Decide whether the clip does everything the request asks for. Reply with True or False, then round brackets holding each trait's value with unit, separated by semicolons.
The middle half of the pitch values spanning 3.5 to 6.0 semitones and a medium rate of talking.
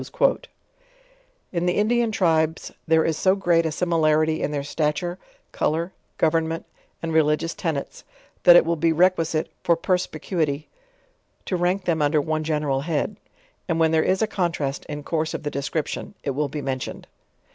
False (2.4 semitones; 165 wpm)